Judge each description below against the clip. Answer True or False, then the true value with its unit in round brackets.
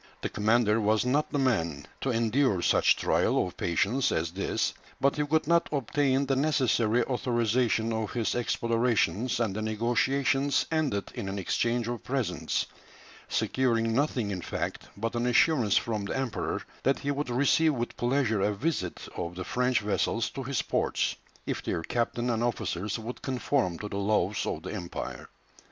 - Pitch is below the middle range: True (120 Hz)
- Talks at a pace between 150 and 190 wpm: True (170 wpm)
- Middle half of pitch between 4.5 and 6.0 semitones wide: False (4.0 semitones)